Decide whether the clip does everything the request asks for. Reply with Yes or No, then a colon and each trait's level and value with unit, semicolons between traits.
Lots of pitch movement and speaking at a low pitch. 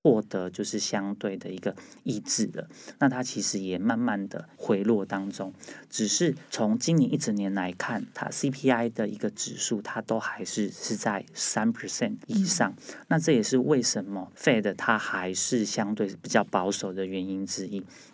Yes: wide, 6.3 semitones; low, 105 Hz